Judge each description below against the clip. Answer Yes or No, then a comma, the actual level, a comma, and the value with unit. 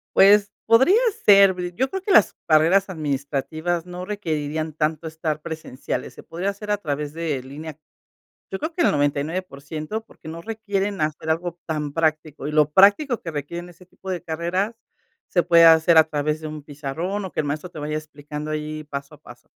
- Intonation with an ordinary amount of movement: Yes, average, 3.8 semitones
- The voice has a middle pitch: Yes, medium, 160 Hz